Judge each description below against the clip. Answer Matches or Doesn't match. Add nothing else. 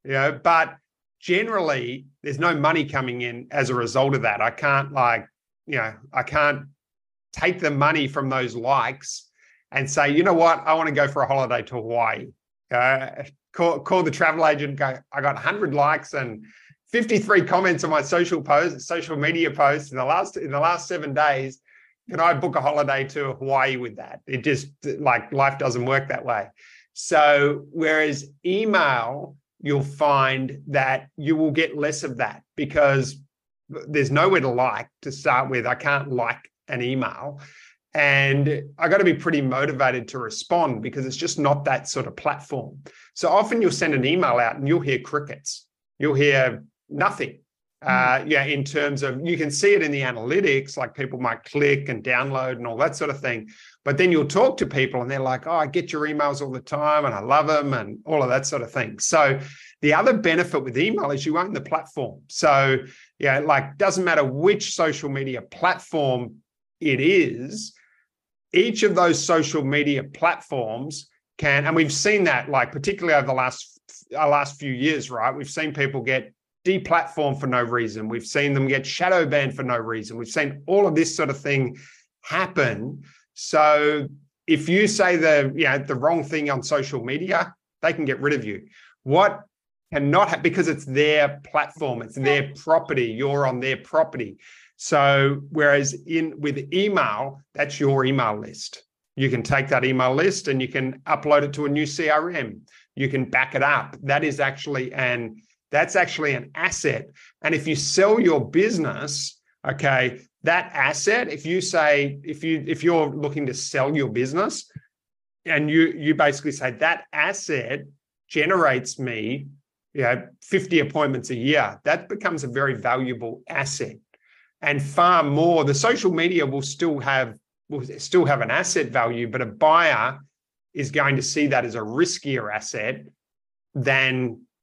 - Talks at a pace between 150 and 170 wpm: Doesn't match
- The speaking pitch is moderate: Matches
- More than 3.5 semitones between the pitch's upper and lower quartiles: Doesn't match